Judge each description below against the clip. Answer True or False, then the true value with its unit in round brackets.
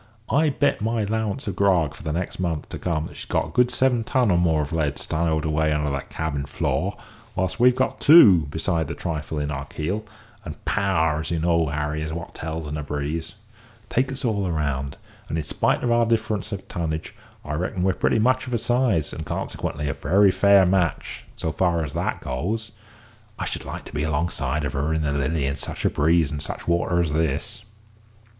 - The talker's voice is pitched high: False (85 Hz)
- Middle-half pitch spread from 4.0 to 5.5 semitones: True (5.2 semitones)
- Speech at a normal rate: False (215 wpm)